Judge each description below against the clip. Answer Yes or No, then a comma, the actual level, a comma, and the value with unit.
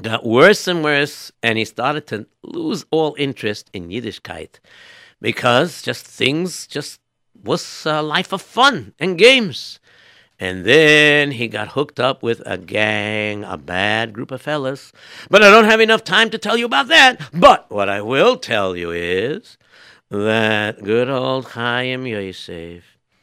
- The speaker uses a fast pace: No, average, 160 wpm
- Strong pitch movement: Yes, wide, 6.8 semitones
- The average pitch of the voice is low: Yes, low, 130 Hz